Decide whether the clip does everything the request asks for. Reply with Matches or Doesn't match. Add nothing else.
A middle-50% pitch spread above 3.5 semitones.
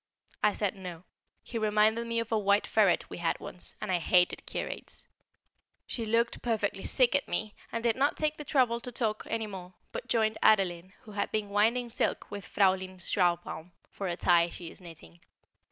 Matches